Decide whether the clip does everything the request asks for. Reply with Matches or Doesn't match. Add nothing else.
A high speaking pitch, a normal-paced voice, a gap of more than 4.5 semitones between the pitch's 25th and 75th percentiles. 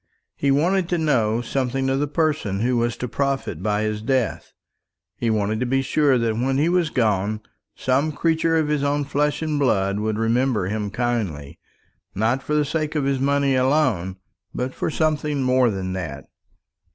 Doesn't match